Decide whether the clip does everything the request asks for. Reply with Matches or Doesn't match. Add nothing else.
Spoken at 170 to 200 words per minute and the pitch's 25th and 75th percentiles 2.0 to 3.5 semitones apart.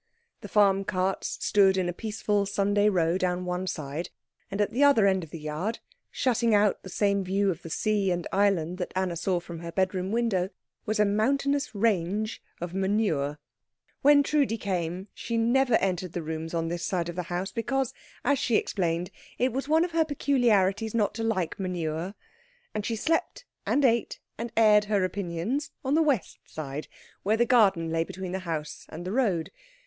Doesn't match